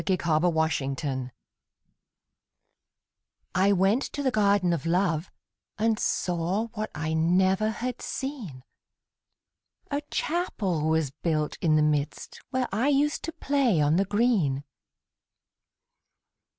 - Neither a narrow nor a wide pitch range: No, wide, 6.1 semitones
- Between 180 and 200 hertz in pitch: Yes, medium, 185 Hz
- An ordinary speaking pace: No, slow, 120 wpm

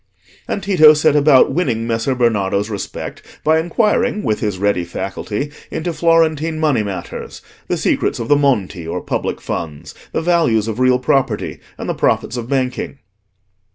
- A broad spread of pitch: Yes, wide, 6.9 semitones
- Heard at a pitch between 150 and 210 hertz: No, low, 130 Hz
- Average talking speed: Yes, average, 155 wpm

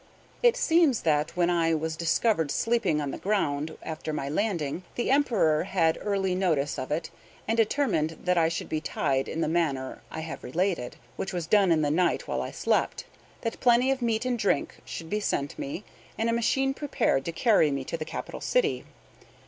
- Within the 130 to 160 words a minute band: No, average, 195 wpm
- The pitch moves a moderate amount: No, wide, 6.4 semitones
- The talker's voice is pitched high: No, medium, 175 Hz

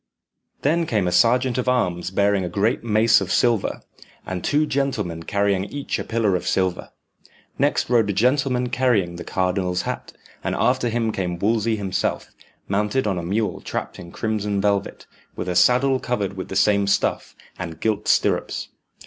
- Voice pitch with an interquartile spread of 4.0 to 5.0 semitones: Yes, average, 4.4 semitones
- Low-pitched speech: Yes, low, 105 Hz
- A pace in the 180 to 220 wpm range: No, average, 170 wpm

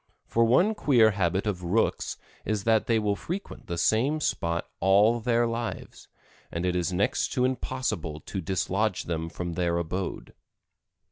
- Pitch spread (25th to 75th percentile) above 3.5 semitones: Yes, average, 4.8 semitones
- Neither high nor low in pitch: No, low, 100 Hz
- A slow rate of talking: No, average, 155 wpm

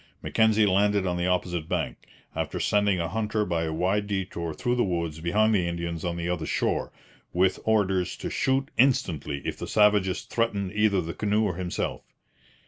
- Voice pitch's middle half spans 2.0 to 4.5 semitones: Yes, average, 3.5 semitones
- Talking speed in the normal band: Yes, average, 180 wpm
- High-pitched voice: No, very low, 95 Hz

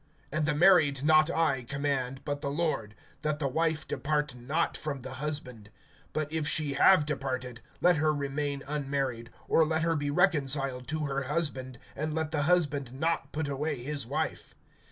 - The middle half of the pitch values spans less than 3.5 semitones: Yes, narrow, 2.4 semitones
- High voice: No, medium, 145 Hz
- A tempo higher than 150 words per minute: Yes, average, 175 wpm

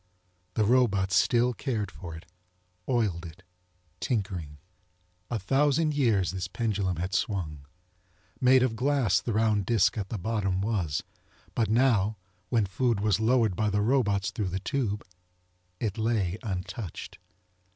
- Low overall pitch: Yes, low, 105 Hz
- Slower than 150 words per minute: Yes, average, 140 wpm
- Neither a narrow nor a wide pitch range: Yes, average, 4.0 semitones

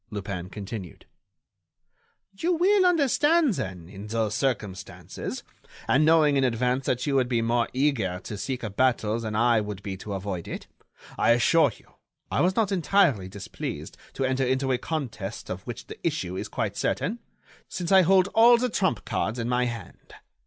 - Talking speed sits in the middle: Yes, average, 175 wpm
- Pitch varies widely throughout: Yes, wide, 8.0 semitones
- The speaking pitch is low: Yes, low, 125 Hz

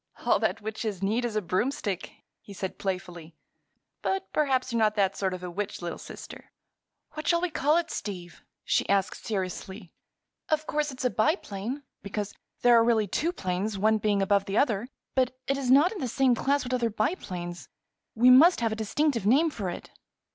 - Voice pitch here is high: Yes, high, 220 Hz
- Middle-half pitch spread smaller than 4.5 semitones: No, wide, 5.6 semitones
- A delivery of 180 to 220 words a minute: Yes, average, 190 wpm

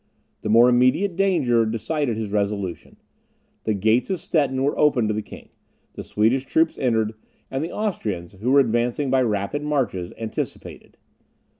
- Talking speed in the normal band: Yes, average, 155 wpm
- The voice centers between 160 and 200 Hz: No, low, 120 Hz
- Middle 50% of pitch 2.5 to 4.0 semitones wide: No, average, 5.0 semitones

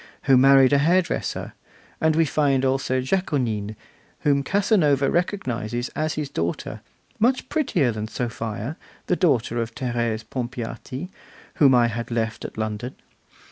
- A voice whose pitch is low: Yes, low, 130 Hz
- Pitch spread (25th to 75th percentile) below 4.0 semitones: No, average, 4.7 semitones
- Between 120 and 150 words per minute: Yes, slow, 135 wpm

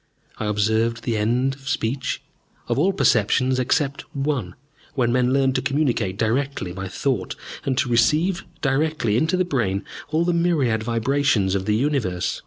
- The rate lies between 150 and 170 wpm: Yes, average, 160 wpm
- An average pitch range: Yes, average, 4.3 semitones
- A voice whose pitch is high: No, low, 125 Hz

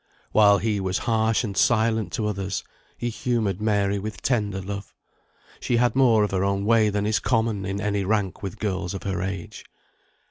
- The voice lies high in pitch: No, low, 105 Hz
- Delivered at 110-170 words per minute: No, average, 185 wpm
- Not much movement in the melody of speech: Yes, narrow, 2.2 semitones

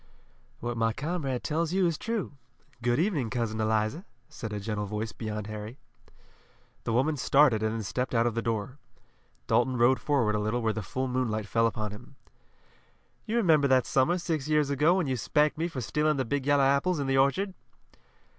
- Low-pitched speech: Yes, low, 130 Hz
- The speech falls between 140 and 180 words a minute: No, average, 195 wpm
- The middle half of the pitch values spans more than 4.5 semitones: Yes, average, 5.2 semitones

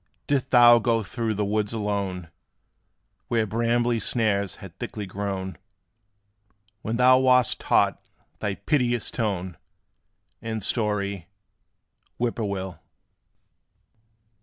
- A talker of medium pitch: No, low, 110 Hz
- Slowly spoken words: Yes, slow, 105 wpm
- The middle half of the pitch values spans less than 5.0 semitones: Yes, average, 3.2 semitones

